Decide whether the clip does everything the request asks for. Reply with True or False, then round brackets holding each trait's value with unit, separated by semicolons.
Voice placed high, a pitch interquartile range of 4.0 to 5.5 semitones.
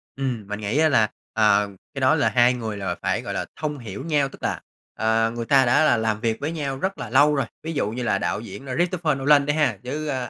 False (130 Hz; 4.7 semitones)